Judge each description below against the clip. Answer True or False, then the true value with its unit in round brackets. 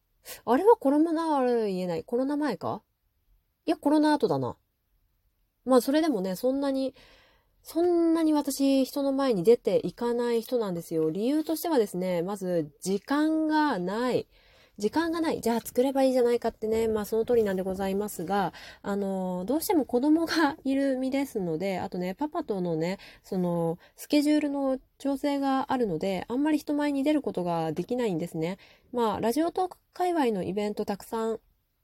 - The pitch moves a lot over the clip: True (7.0 semitones)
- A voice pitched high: True (245 Hz)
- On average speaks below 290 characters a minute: False (355 characters per minute)